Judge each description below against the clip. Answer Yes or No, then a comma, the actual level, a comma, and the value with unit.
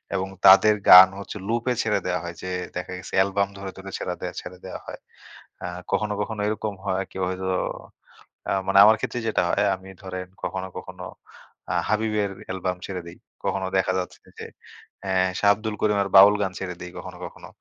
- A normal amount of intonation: No, narrow, 2.0 semitones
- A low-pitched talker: Yes, very low, 95 Hz